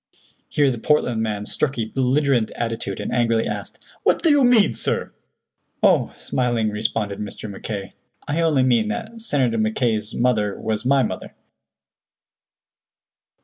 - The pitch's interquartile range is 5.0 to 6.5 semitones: No, average, 4.1 semitones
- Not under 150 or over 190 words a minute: No, average, 140 wpm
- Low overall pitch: Yes, low, 120 Hz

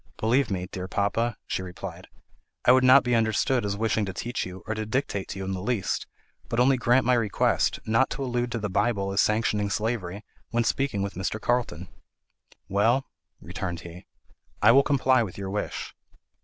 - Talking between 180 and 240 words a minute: Yes, average, 190 wpm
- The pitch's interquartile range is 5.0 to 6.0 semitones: No, average, 3.9 semitones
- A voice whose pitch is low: Yes, low, 110 Hz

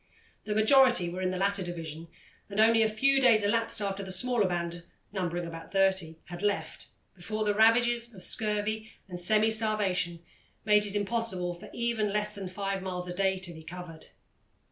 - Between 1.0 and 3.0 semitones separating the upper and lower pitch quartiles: No, average, 3.5 semitones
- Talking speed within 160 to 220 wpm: Yes, average, 180 wpm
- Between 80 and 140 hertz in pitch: No, high, 200 Hz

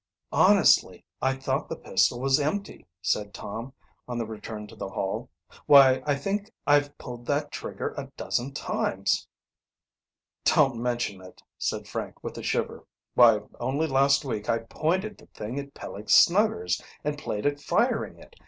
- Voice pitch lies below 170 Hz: Yes, low, 135 Hz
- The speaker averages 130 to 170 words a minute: Yes, average, 160 wpm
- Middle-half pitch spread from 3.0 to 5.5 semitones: Yes, average, 4.2 semitones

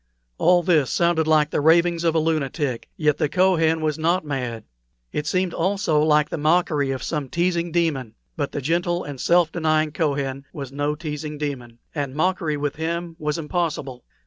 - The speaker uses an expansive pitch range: No, average, 2.8 semitones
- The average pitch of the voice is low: No, medium, 155 Hz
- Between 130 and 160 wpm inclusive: No, average, 175 wpm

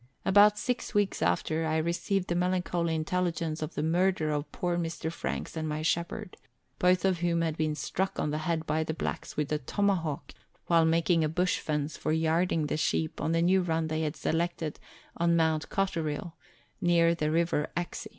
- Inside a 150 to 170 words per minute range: No, average, 190 wpm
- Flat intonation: Yes, narrow, 2.1 semitones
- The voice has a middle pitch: Yes, medium, 165 Hz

